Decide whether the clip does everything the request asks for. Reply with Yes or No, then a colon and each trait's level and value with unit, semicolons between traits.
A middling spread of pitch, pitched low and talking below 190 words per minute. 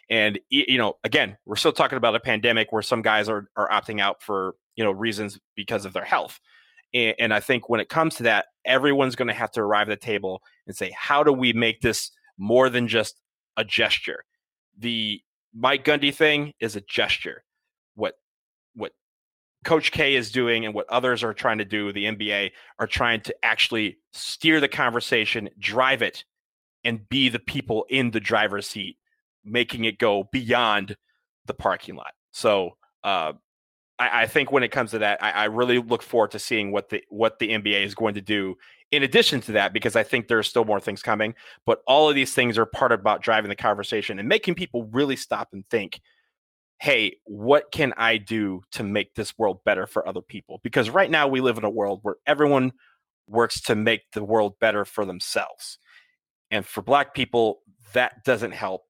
No: average, 4.1 semitones; low, 120 Hz; average, 200 wpm